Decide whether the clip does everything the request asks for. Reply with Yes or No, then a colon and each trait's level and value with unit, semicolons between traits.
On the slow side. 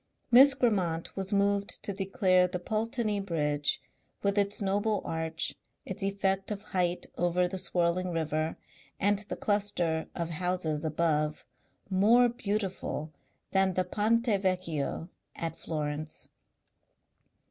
Yes: slow, 120 wpm